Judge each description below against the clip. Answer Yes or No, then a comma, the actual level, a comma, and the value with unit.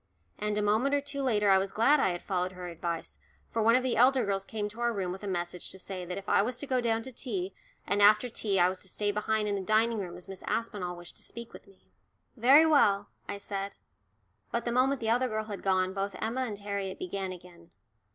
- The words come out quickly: Yes, fast, 250 wpm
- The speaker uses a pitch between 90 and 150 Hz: No, high, 205 Hz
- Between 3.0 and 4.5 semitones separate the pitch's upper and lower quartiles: Yes, average, 3.7 semitones